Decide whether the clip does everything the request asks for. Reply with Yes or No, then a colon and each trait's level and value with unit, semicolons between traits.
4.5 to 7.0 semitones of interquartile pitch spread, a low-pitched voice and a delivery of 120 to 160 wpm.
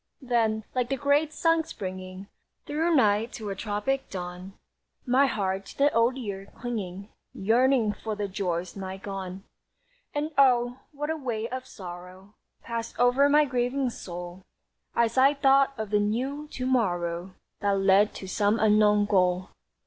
No: average, 5.3 semitones; high, 220 Hz; average, 155 wpm